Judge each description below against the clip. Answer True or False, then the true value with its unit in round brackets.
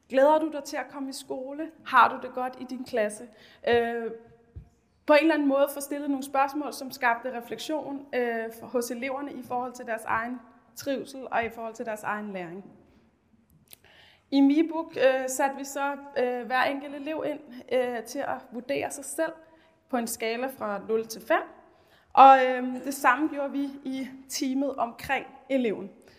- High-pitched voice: True (265 Hz)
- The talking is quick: False (165 wpm)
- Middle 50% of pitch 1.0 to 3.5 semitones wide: True (2.9 semitones)